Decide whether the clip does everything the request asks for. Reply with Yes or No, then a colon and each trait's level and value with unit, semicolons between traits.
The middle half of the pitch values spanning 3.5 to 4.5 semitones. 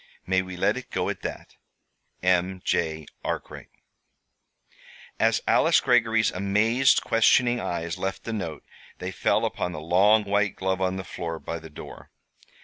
Yes: average, 3.9 semitones